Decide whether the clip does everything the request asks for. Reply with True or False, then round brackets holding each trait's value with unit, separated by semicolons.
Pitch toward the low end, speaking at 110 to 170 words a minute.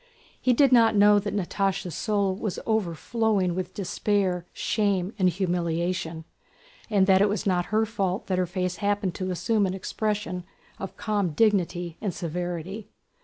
False (190 Hz; 155 wpm)